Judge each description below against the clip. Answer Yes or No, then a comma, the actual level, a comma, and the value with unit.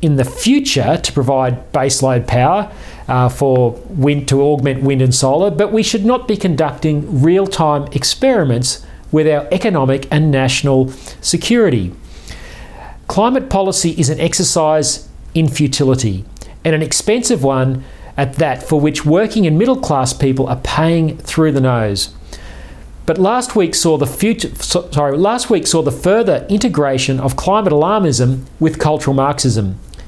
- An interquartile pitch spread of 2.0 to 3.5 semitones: No, average, 4.6 semitones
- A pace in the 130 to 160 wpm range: Yes, average, 145 wpm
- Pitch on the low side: No, medium, 150 Hz